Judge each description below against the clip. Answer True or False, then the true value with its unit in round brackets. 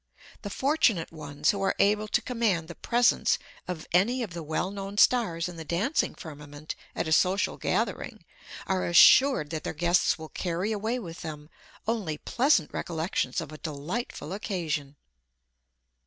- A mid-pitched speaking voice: True (175 Hz)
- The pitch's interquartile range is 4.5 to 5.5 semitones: True (5.0 semitones)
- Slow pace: False (155 wpm)